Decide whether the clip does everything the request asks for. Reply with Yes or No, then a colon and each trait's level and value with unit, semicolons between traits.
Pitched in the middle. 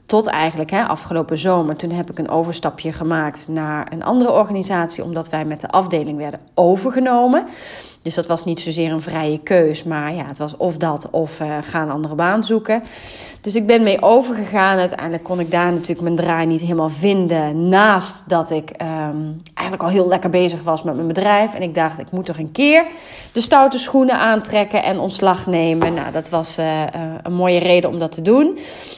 Yes: medium, 170 Hz